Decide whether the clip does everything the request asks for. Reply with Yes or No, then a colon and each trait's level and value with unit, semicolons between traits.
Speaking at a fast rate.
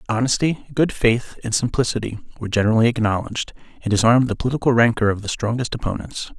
No: average, 170 wpm